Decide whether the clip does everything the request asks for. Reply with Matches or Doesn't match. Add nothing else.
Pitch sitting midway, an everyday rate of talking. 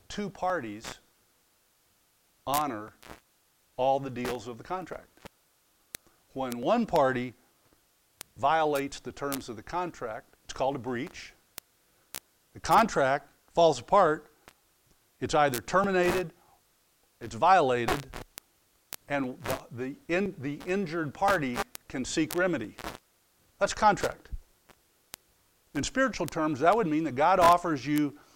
Doesn't match